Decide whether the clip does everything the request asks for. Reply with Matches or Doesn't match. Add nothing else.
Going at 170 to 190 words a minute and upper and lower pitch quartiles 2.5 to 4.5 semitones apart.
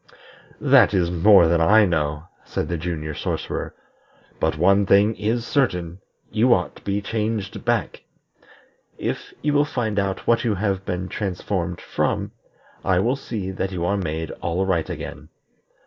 Doesn't match